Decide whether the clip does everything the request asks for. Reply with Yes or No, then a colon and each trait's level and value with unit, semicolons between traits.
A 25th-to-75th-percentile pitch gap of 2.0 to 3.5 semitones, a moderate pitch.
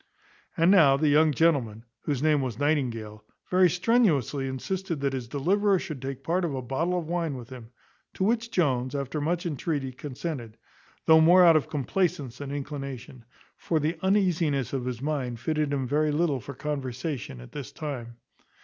No: average, 4.2 semitones; medium, 145 Hz